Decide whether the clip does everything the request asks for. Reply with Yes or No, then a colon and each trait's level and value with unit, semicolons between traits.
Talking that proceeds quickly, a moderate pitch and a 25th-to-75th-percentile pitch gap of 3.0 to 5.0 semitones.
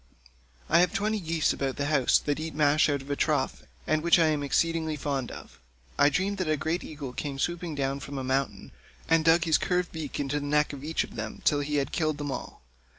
No: fast, 235 wpm; medium, 150 Hz; narrow, 2.6 semitones